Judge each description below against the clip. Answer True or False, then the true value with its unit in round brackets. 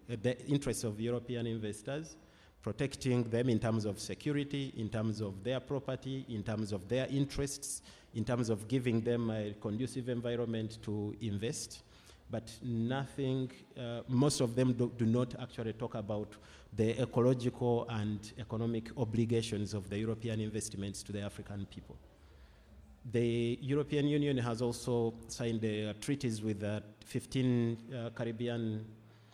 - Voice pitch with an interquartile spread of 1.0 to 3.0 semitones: True (2.7 semitones)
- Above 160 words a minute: False (145 wpm)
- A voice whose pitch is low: True (115 Hz)